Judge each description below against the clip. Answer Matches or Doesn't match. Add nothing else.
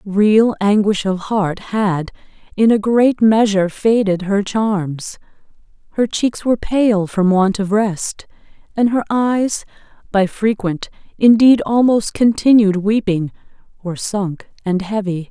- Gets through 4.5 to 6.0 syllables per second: Doesn't match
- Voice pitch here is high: Matches